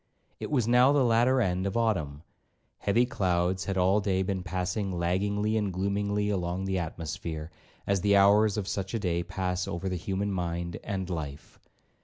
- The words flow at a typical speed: Yes, average, 175 wpm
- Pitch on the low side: Yes, very low, 95 Hz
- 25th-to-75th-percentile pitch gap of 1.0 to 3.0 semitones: Yes, narrow, 2.6 semitones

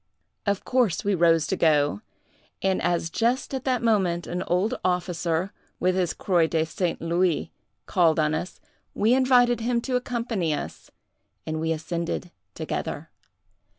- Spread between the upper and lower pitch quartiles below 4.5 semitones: No, wide, 5.6 semitones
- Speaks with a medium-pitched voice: Yes, medium, 180 Hz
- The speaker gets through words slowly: No, average, 150 wpm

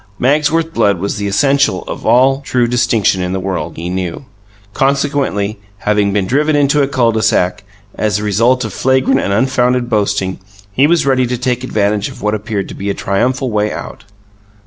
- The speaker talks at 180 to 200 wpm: Yes, average, 190 wpm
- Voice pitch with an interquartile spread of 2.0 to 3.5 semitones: No, average, 4.7 semitones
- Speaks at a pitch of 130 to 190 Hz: No, low, 115 Hz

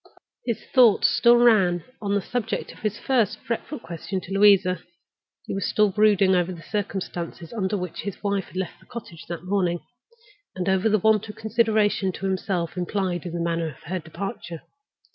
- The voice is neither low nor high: No, high, 195 Hz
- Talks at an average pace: Yes, average, 180 wpm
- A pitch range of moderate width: Yes, average, 3.3 semitones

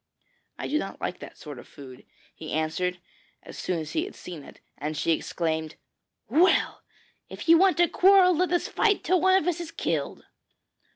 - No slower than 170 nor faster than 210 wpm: Yes, average, 190 wpm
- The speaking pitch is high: Yes, very high, 300 Hz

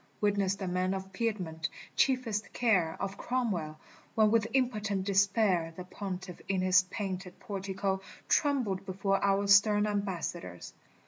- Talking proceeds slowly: Yes, slow, 130 wpm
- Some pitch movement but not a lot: No, narrow, 2.1 semitones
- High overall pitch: Yes, high, 195 Hz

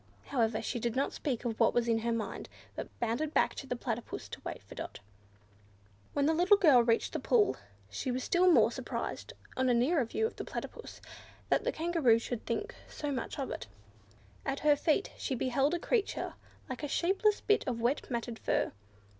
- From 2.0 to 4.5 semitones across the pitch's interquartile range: No, average, 5.2 semitones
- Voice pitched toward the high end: Yes, very high, 260 Hz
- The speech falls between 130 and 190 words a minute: No, average, 200 wpm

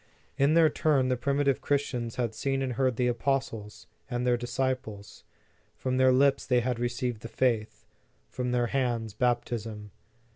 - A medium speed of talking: Yes, average, 155 wpm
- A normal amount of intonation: No, narrow, 2.3 semitones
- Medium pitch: No, low, 125 Hz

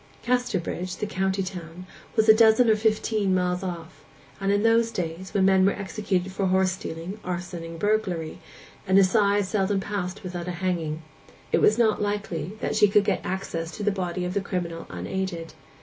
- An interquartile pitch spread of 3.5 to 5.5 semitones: No, narrow, 2.6 semitones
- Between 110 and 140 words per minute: No, average, 185 wpm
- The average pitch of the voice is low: No, high, 190 Hz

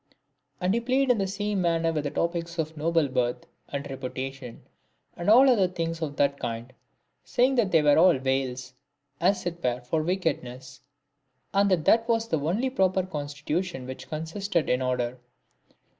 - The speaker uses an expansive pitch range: Yes, wide, 6.0 semitones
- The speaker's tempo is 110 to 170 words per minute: Yes, average, 165 wpm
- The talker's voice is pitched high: No, medium, 165 Hz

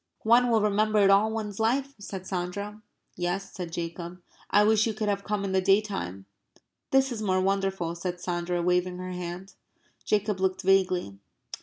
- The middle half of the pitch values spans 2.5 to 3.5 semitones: Yes, average, 2.8 semitones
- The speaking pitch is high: Yes, high, 195 Hz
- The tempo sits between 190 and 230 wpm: No, average, 175 wpm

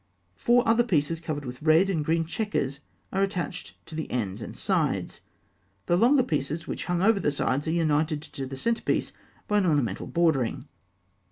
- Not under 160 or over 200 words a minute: Yes, average, 180 wpm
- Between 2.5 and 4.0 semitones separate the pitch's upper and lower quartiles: No, average, 5.1 semitones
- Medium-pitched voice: Yes, medium, 160 Hz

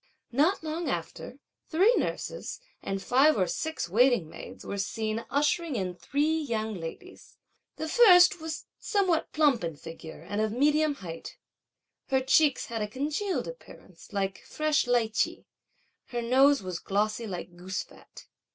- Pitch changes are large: Yes, wide, 7.5 semitones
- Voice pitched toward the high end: Yes, very high, 250 Hz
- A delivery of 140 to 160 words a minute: Yes, average, 150 wpm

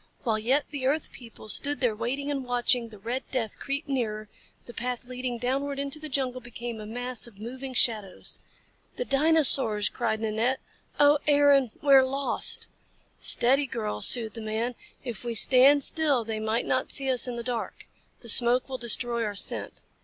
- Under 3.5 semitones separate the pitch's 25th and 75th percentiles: Yes, average, 3.1 semitones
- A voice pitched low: No, high, 245 Hz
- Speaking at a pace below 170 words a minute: No, average, 180 wpm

